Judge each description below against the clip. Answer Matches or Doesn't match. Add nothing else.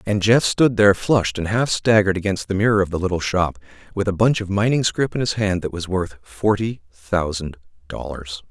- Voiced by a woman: Doesn't match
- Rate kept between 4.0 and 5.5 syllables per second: Matches